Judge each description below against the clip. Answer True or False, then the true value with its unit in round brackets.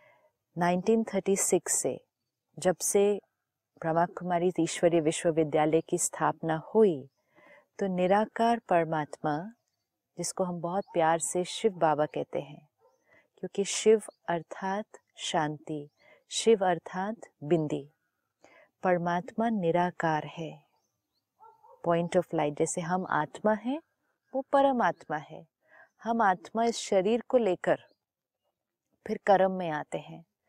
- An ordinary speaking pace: False (105 wpm)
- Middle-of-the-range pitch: True (180 Hz)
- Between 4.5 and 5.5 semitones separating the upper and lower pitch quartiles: True (4.9 semitones)